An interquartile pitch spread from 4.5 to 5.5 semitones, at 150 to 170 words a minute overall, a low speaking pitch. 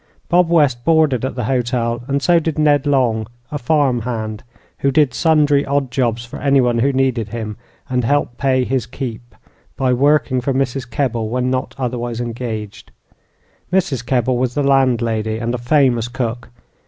No: average, 2.8 semitones; average, 165 wpm; low, 125 Hz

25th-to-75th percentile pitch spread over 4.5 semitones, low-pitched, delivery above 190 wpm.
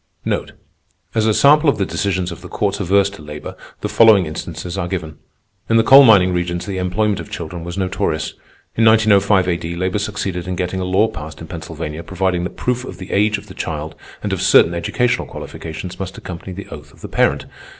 No: average, 3.2 semitones; very low, 95 Hz; fast, 205 wpm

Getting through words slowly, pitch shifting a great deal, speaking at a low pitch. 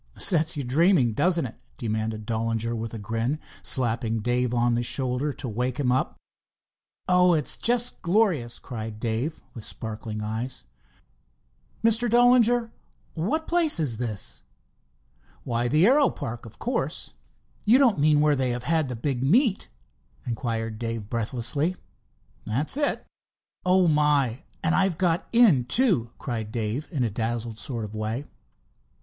No: average, 145 wpm; wide, 7.0 semitones; low, 125 Hz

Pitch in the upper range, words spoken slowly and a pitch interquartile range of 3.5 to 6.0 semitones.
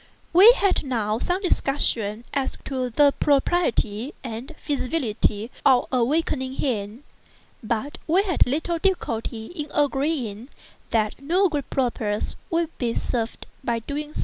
Yes: very high, 265 Hz; slow, 130 wpm; average, 5.1 semitones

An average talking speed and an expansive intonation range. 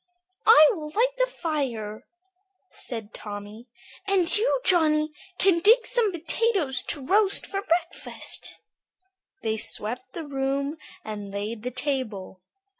No: slow, 120 wpm; wide, 8.7 semitones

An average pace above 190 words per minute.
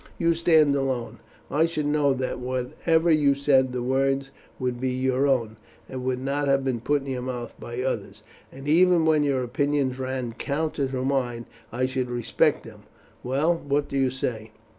No: average, 185 wpm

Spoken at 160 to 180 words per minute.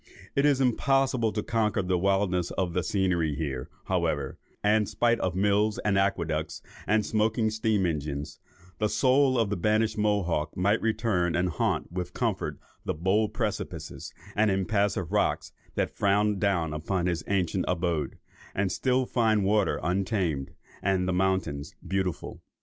No: average, 150 wpm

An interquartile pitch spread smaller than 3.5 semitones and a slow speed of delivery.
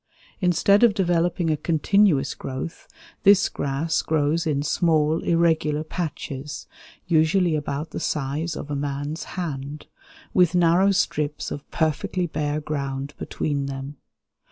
Yes: average, 3.0 semitones; slow, 125 wpm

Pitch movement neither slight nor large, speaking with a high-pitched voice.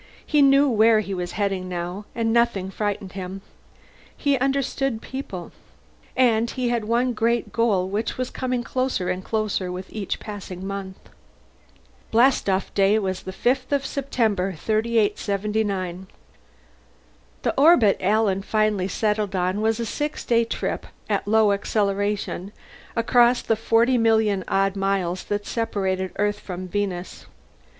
Yes: average, 3.4 semitones; high, 210 Hz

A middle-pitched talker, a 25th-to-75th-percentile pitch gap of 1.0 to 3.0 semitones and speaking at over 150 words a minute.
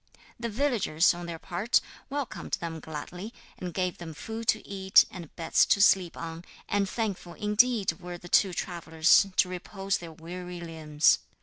No: medium, 180 Hz; average, 3.4 semitones; average, 165 wpm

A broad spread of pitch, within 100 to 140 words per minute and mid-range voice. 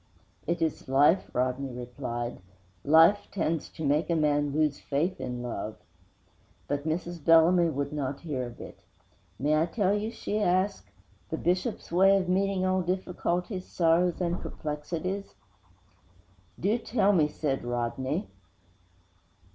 No: average, 4.6 semitones; slow, 135 wpm; medium, 165 Hz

